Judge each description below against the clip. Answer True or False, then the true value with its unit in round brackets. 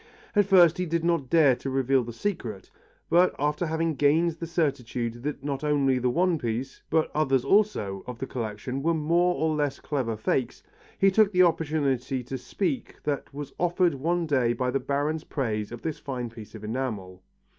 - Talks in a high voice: False (140 Hz)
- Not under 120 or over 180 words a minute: False (190 wpm)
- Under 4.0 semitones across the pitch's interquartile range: False (4.9 semitones)